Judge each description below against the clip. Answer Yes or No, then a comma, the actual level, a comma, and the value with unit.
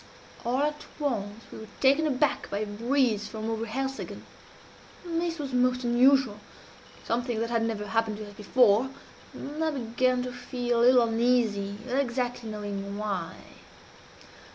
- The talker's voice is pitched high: Yes, high, 240 Hz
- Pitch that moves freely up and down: No, average, 3.3 semitones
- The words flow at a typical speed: Yes, average, 155 wpm